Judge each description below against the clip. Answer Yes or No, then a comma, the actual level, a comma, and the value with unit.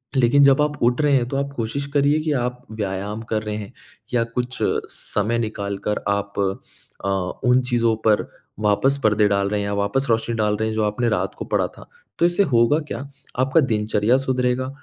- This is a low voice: Yes, low, 115 Hz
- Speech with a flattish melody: No, average, 4.0 semitones